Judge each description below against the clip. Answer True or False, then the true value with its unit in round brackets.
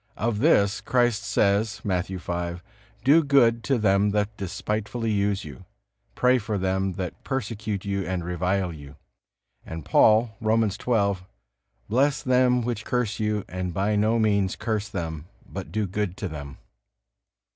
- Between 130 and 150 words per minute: True (145 wpm)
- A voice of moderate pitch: False (105 Hz)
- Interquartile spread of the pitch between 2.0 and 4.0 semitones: True (3.3 semitones)